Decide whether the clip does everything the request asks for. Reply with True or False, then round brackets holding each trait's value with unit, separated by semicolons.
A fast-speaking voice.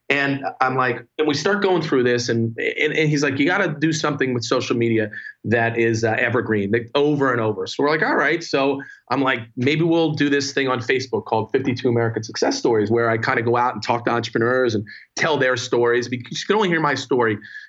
True (240 wpm)